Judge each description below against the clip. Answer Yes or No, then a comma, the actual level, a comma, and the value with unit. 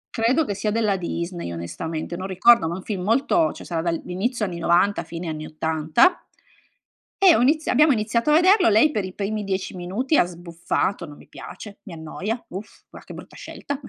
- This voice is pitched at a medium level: No, high, 195 Hz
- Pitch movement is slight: No, wide, 5.6 semitones